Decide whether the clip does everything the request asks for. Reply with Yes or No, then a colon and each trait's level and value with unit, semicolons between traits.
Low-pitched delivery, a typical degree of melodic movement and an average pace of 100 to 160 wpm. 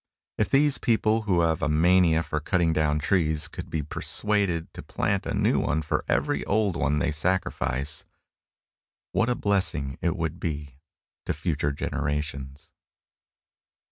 Yes: very low, 80 Hz; average, 4.1 semitones; average, 150 wpm